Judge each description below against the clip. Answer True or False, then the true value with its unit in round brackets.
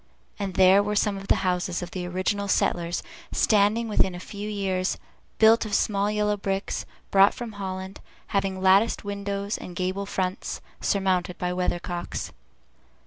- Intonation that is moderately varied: False (1.7 semitones)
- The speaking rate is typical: True (150 wpm)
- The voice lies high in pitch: True (195 Hz)